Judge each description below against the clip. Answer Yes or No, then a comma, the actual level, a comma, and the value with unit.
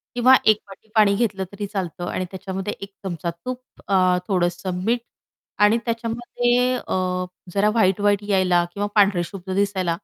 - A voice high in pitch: Yes, high, 195 Hz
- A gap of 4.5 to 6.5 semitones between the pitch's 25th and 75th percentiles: No, average, 2.8 semitones